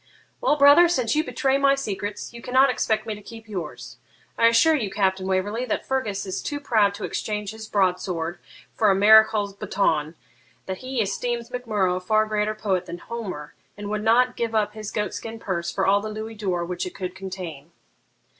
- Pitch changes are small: No, average, 3.3 semitones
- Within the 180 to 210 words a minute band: Yes, average, 200 wpm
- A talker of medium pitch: No, high, 210 Hz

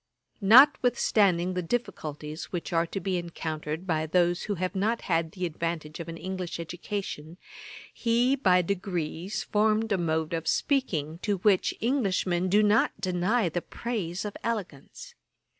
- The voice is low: No, medium, 185 Hz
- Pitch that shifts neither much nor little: Yes, average, 4.0 semitones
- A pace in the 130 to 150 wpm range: Yes, average, 145 wpm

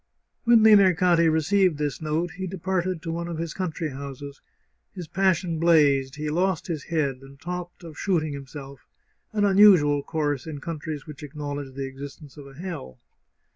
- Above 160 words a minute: Yes, average, 175 wpm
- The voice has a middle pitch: Yes, medium, 160 Hz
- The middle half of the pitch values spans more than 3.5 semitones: Yes, average, 3.9 semitones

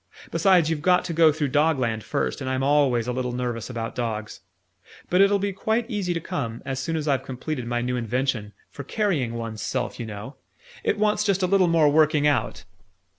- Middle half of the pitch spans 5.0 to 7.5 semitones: Yes, wide, 5.6 semitones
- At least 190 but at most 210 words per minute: Yes, fast, 205 wpm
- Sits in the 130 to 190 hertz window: Yes, medium, 140 Hz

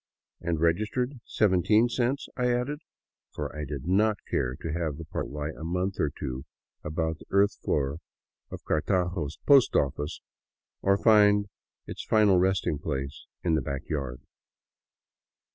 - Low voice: Yes, very low, 85 Hz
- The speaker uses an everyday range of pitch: No, wide, 5.9 semitones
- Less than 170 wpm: Yes, average, 145 wpm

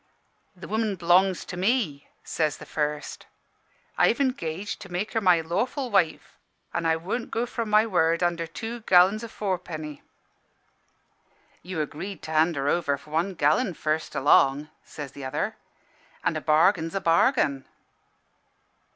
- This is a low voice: No, medium, 175 Hz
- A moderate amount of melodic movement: Yes, average, 4.6 semitones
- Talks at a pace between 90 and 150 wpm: Yes, average, 145 wpm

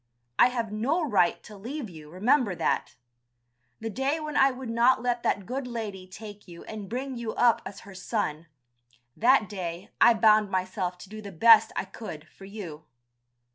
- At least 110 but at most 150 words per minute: No, average, 180 wpm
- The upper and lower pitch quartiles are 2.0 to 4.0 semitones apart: No, average, 4.4 semitones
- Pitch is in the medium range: No, high, 215 Hz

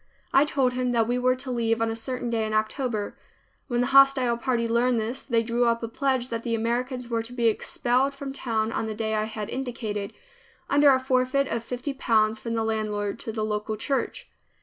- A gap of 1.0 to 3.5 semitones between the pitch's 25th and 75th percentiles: Yes, narrow, 2.4 semitones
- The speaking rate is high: Yes, fast, 215 wpm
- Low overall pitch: No, high, 235 Hz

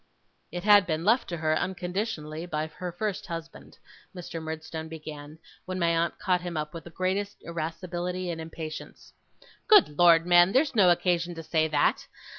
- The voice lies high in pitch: No, medium, 170 Hz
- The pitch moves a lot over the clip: No, narrow, 2.4 semitones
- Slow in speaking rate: No, average, 170 wpm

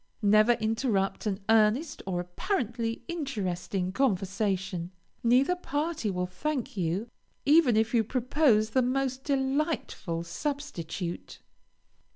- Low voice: No, high, 225 Hz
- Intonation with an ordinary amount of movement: No, wide, 6.0 semitones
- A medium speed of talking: No, slow, 105 wpm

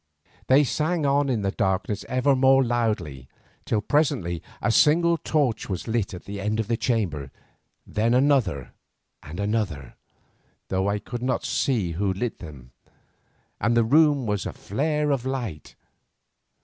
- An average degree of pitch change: No, wide, 5.8 semitones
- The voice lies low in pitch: Yes, low, 115 Hz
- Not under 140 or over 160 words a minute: Yes, average, 150 wpm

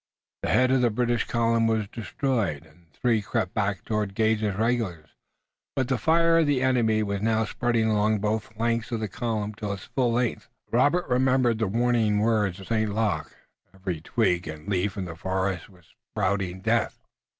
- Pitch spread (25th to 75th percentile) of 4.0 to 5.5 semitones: No, average, 3.3 semitones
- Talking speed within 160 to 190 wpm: Yes, average, 185 wpm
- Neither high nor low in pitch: No, low, 110 Hz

